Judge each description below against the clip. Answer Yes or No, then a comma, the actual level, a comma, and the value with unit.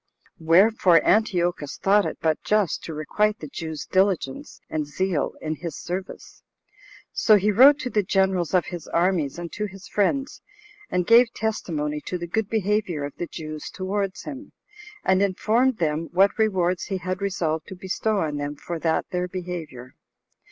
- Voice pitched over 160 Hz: Yes, medium, 185 Hz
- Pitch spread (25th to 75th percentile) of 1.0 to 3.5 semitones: No, average, 4.2 semitones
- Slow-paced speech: No, average, 165 wpm